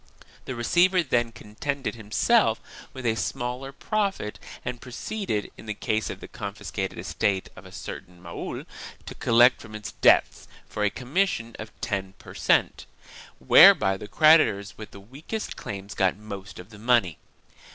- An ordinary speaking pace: Yes, average, 155 wpm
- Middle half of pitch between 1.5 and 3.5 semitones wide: No, average, 4.4 semitones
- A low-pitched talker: Yes, low, 110 Hz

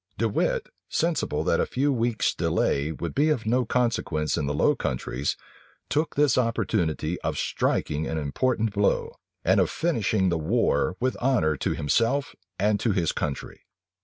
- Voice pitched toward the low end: Yes, low, 110 Hz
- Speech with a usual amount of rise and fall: No, wide, 8.6 semitones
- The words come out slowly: No, average, 160 wpm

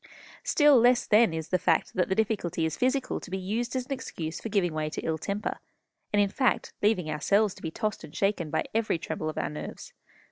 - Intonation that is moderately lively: No, wide, 5.7 semitones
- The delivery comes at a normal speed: No, fast, 225 wpm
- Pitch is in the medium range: No, high, 195 Hz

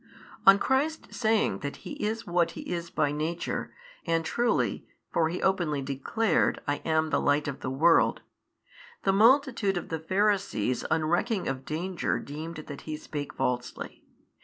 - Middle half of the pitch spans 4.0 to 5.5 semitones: Yes, average, 5.1 semitones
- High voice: No, medium, 165 Hz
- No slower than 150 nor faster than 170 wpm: Yes, average, 155 wpm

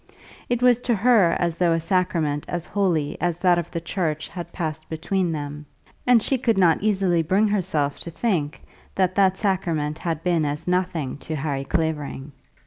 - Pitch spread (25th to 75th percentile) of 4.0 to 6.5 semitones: No, average, 3.5 semitones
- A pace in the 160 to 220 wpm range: Yes, average, 180 wpm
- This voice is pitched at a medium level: Yes, medium, 170 Hz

